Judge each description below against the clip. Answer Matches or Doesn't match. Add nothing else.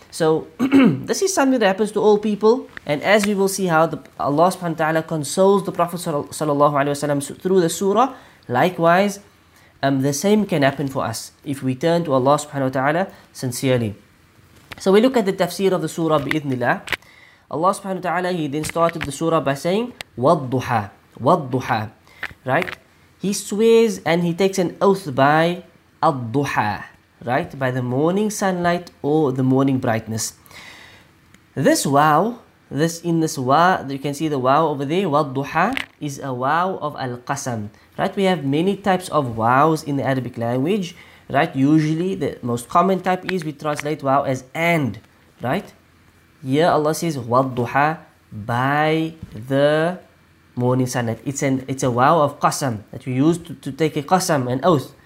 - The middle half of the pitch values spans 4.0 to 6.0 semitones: Matches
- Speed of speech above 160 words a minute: Matches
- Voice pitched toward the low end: Doesn't match